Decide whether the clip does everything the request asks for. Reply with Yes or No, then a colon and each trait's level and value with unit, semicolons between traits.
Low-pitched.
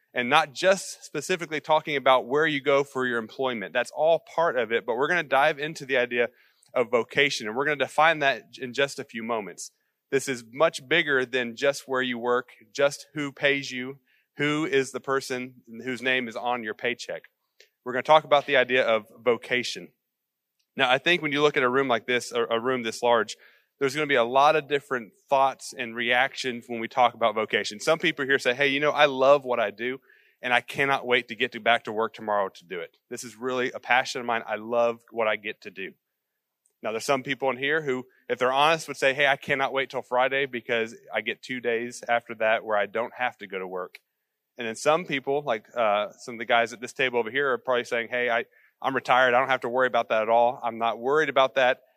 Yes: low, 130 Hz